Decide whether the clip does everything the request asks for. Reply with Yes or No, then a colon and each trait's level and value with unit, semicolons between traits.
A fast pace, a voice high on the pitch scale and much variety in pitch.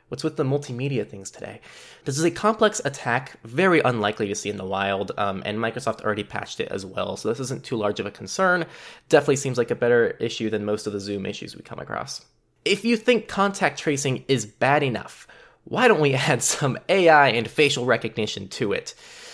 No: fast, 210 wpm; low, 135 Hz; wide, 7.4 semitones